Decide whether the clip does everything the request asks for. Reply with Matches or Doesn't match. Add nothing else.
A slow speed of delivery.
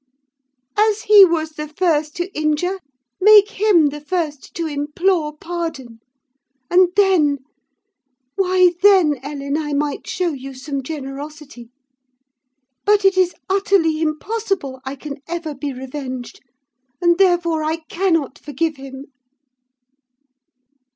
Matches